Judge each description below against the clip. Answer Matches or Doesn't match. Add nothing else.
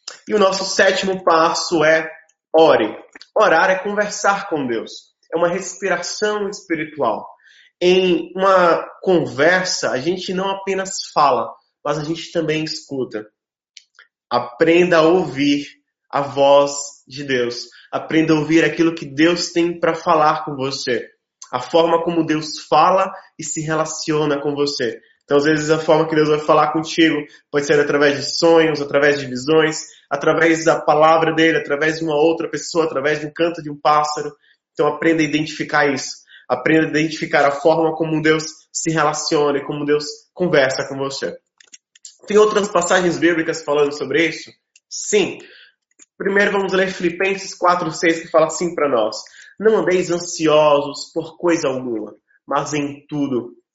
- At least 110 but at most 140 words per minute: Doesn't match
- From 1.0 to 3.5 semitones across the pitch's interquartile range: Matches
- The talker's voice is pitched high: Doesn't match